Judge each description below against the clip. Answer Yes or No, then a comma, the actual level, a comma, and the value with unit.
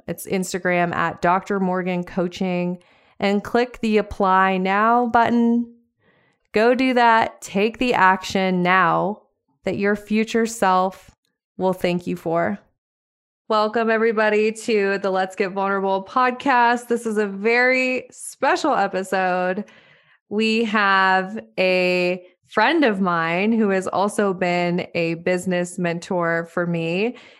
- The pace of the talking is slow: Yes, slow, 125 wpm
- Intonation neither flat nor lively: Yes, average, 3.7 semitones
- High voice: Yes, high, 195 Hz